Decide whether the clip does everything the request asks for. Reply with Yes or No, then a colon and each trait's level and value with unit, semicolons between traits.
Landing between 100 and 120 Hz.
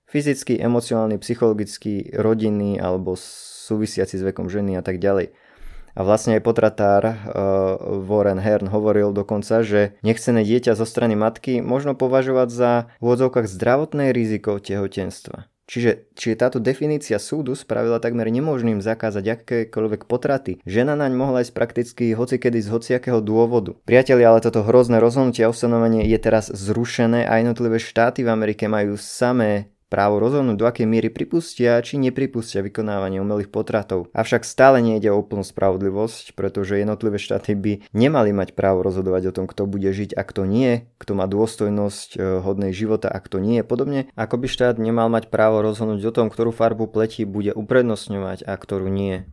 Yes: low, 110 Hz